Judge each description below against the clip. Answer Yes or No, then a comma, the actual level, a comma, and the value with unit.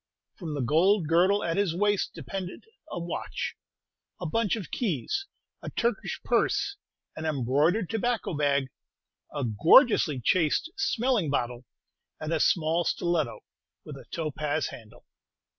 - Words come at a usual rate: No, slow, 130 wpm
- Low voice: No, medium, 170 Hz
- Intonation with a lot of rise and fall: Yes, wide, 5.7 semitones